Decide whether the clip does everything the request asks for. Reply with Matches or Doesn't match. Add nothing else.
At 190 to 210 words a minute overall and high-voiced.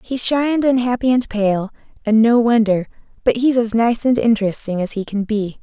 Matches